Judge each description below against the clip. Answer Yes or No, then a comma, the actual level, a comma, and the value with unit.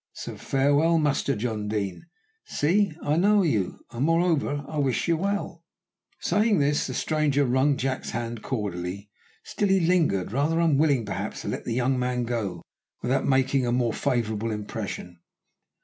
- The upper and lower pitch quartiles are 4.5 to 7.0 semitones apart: Yes, wide, 5.6 semitones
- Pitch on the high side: No, low, 135 Hz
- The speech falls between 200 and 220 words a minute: No, average, 160 wpm